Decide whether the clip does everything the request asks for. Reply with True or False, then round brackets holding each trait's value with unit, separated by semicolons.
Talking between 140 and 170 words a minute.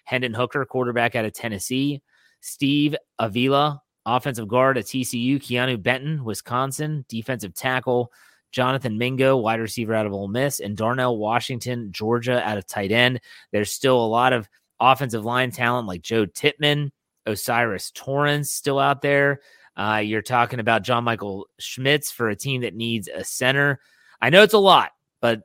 True (165 wpm)